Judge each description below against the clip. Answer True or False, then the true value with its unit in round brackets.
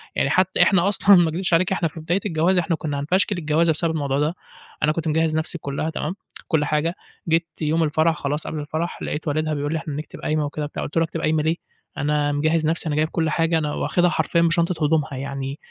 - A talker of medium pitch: True (160 Hz)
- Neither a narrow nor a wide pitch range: False (1.9 semitones)